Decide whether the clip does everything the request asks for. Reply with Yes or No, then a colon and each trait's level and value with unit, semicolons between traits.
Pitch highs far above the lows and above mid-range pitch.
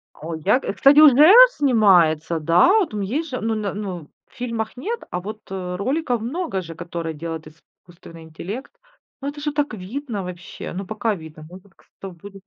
Yes: wide, 6.8 semitones; high, 200 Hz